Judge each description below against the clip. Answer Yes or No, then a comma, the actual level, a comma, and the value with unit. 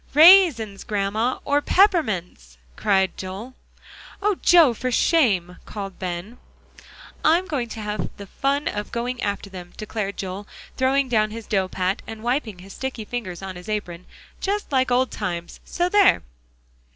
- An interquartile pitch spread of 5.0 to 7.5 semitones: Yes, wide, 5.6 semitones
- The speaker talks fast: No, average, 150 wpm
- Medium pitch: No, high, 215 Hz